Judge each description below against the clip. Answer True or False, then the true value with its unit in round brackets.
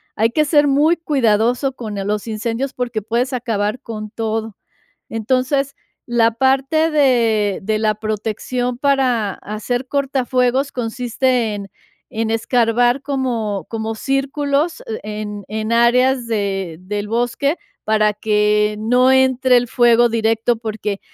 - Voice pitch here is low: False (235 Hz)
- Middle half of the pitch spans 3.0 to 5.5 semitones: True (3.3 semitones)